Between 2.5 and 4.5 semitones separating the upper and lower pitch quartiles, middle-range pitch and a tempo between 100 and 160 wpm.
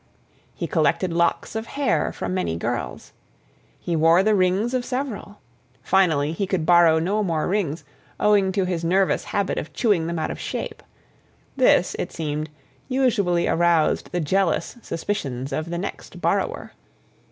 Yes: average, 3.8 semitones; medium, 180 Hz; average, 150 wpm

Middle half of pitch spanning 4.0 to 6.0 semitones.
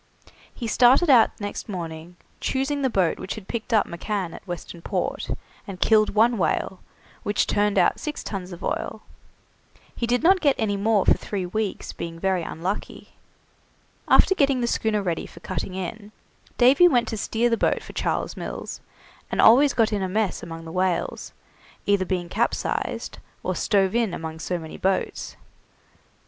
Yes: average, 4.5 semitones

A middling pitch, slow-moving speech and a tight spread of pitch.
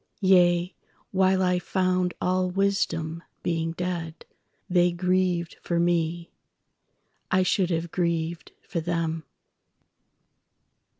Yes: medium, 175 Hz; slow, 95 wpm; narrow, 1.6 semitones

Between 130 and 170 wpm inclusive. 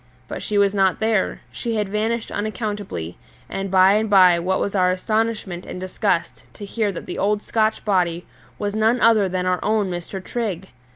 No: average, 185 wpm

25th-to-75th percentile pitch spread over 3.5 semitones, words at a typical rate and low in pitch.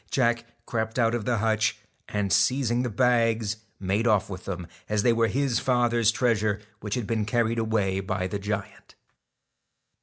No: narrow, 2.5 semitones; average, 170 wpm; low, 110 Hz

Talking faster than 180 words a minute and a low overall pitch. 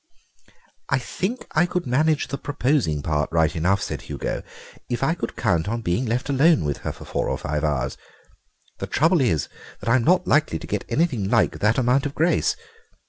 Yes: average, 195 wpm; low, 125 Hz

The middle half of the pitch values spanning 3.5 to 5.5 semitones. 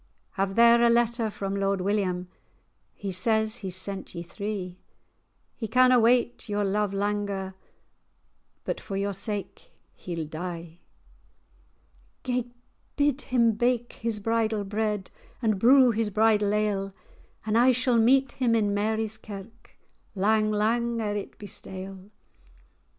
No: average, 3.0 semitones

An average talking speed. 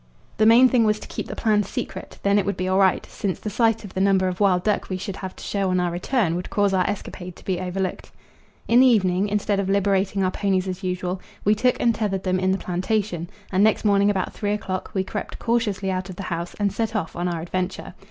No: fast, 250 wpm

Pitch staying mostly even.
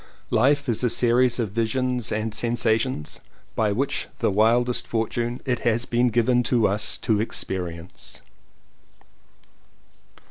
Yes: narrow, 2.1 semitones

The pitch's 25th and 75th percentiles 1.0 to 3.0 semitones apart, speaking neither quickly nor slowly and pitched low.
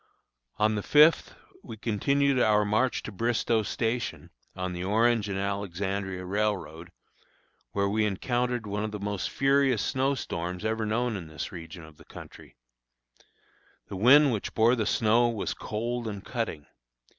No: average, 3.4 semitones; average, 155 wpm; low, 105 Hz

